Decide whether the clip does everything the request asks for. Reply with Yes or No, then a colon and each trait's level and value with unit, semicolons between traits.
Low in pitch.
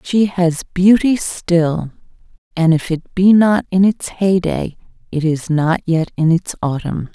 No: medium, 175 Hz